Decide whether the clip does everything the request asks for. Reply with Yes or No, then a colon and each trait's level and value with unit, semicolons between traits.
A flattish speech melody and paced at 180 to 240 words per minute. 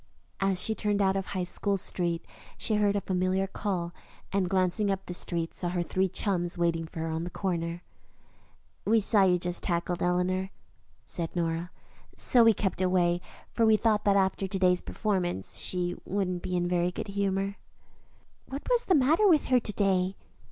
Yes: narrow, 2.3 semitones; average, 190 wpm